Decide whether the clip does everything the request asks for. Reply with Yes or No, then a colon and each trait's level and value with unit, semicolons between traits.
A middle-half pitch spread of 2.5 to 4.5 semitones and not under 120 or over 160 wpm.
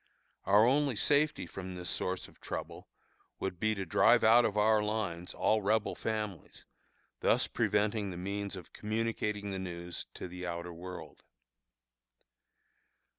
Yes: average, 3.1 semitones; average, 140 wpm